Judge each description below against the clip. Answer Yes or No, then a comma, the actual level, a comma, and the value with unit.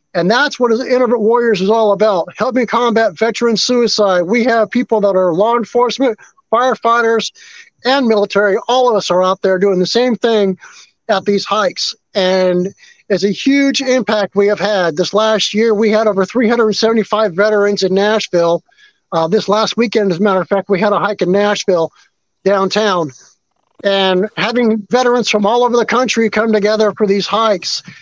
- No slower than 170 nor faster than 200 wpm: Yes, average, 175 wpm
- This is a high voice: Yes, high, 215 Hz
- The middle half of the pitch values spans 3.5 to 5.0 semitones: No, average, 3.0 semitones